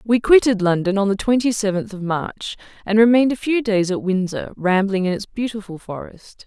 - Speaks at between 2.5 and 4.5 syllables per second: No, 5.3 syllables/s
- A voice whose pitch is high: Yes, high, 205 Hz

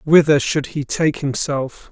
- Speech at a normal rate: Yes, average, 155 wpm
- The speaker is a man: Yes, male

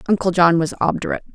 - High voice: No, medium, 175 Hz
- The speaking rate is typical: Yes, average, 180 wpm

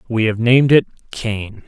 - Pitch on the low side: Yes, low, 115 Hz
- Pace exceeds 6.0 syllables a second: No, 4.8 syllables/s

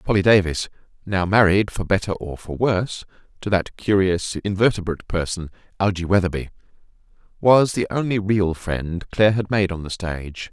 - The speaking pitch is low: Yes, very low, 95 Hz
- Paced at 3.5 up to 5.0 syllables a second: No, 5.2 syllables/s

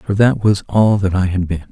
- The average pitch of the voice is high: No, low, 100 Hz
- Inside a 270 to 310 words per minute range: Yes, fast, 280 wpm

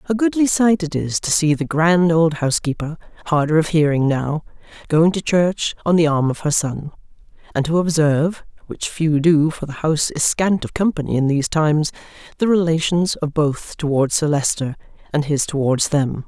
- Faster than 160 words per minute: Yes, average, 180 wpm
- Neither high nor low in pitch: Yes, medium, 160 Hz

